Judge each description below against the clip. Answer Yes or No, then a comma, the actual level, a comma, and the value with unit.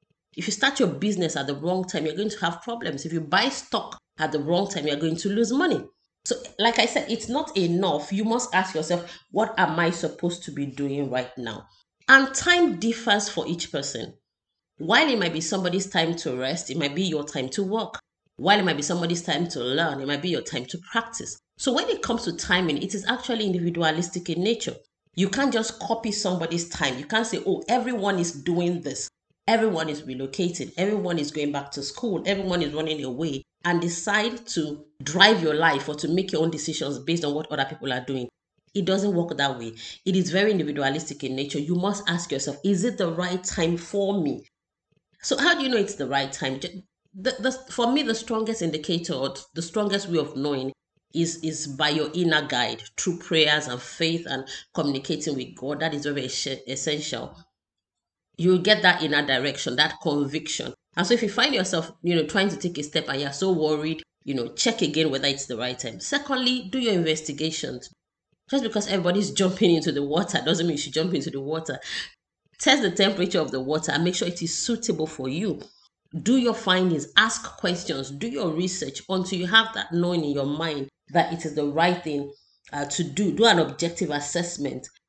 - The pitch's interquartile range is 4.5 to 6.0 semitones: Yes, average, 5.0 semitones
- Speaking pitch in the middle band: Yes, medium, 170 Hz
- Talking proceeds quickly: Yes, fast, 210 wpm